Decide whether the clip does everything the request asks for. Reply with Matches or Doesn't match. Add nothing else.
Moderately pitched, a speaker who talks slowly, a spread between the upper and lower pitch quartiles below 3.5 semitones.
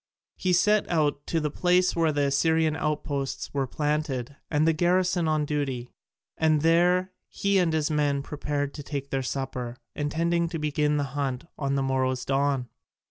Doesn't match